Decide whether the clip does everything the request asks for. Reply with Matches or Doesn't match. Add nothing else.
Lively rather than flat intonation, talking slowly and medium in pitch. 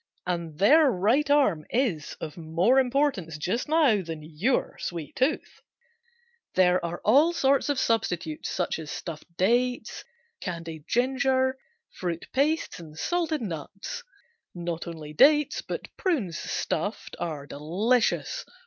Doesn't match